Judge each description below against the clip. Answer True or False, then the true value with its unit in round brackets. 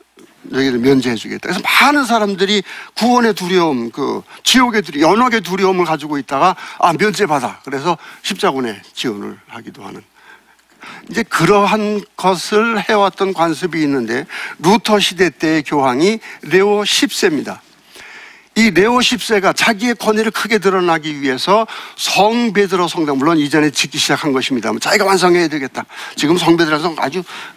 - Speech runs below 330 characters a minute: False (335 characters per minute)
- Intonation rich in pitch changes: True (5.7 semitones)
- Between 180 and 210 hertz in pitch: True (190 Hz)